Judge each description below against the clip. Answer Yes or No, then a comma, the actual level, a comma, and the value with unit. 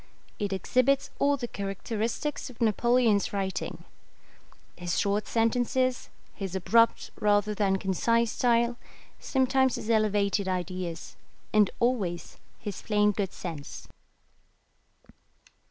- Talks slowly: Yes, slow, 105 wpm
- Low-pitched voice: No, high, 210 Hz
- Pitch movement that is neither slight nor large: Yes, average, 3.6 semitones